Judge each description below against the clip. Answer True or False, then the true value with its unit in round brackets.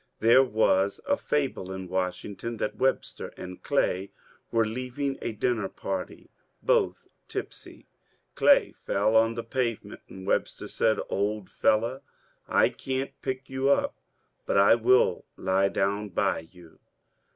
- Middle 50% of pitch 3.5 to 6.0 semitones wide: True (4.8 semitones)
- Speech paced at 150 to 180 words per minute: False (140 wpm)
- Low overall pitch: True (110 Hz)